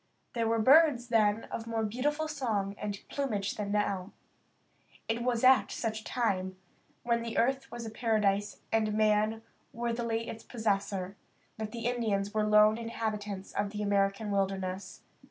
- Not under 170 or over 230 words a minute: No, average, 150 wpm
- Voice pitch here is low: No, high, 220 Hz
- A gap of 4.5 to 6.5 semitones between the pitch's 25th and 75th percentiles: No, narrow, 2.4 semitones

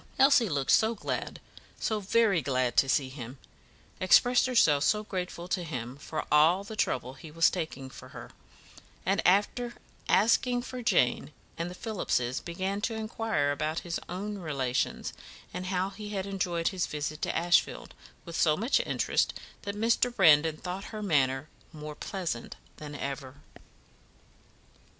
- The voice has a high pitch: No, medium, 175 Hz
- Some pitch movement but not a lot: No, wide, 5.9 semitones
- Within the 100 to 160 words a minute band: Yes, average, 150 wpm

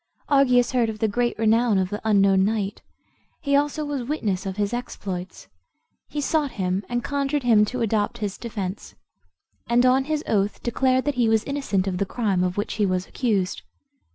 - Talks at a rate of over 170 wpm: Yes, average, 185 wpm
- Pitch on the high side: Yes, high, 225 Hz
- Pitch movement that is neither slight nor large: Yes, average, 4.4 semitones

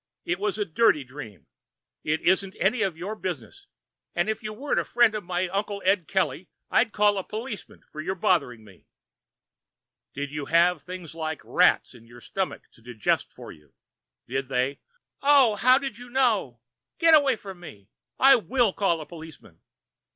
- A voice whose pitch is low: No, medium, 185 Hz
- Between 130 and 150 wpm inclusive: No, average, 180 wpm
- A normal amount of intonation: No, wide, 6.4 semitones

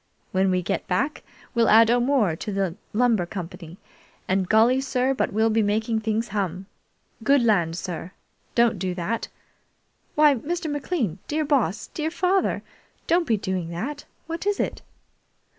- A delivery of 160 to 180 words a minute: No, average, 150 wpm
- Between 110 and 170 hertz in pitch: No, high, 225 Hz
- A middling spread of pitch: No, wide, 6.6 semitones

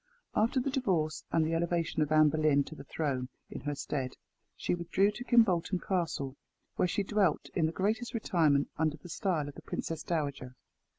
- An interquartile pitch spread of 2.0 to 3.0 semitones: No, average, 4.5 semitones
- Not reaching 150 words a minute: No, average, 185 wpm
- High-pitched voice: No, medium, 165 Hz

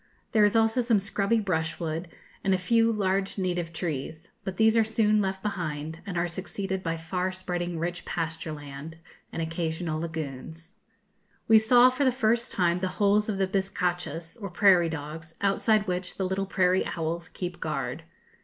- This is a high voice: No, medium, 180 Hz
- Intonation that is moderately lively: Yes, average, 3.5 semitones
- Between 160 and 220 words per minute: Yes, average, 170 wpm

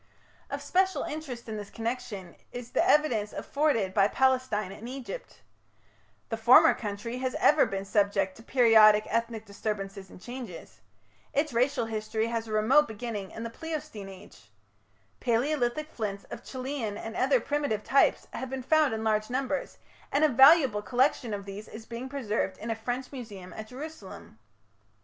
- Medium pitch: No, high, 230 Hz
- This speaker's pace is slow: No, average, 160 wpm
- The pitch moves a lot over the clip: No, average, 4.0 semitones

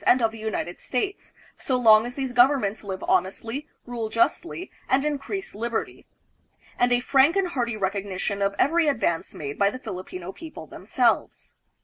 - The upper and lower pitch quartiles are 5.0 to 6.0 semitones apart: Yes, average, 5.3 semitones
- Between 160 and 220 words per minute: Yes, average, 165 wpm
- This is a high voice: Yes, high, 235 Hz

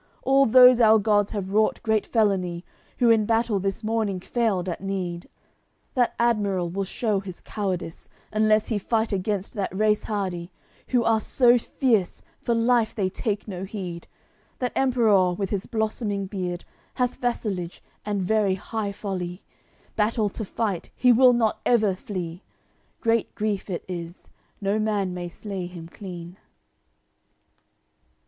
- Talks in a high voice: Yes, high, 205 Hz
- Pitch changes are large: No, average, 3.2 semitones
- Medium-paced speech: Yes, average, 145 wpm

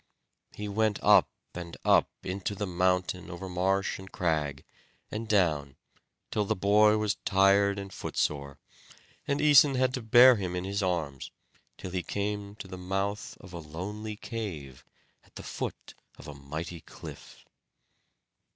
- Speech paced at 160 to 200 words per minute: No, average, 150 wpm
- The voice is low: Yes, very low, 95 Hz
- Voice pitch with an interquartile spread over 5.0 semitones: No, average, 3.2 semitones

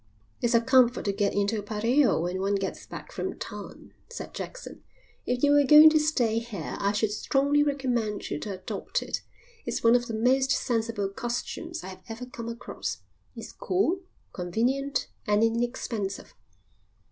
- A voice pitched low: No, high, 235 Hz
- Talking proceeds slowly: No, average, 170 wpm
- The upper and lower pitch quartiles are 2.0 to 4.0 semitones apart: No, average, 4.7 semitones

